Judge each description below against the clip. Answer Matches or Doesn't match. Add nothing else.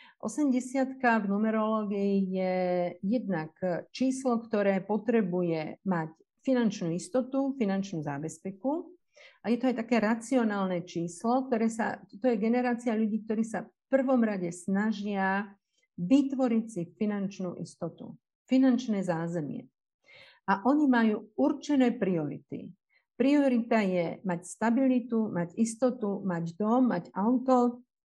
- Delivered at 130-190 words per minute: Doesn't match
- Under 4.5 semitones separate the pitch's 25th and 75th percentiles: Doesn't match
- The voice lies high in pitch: Matches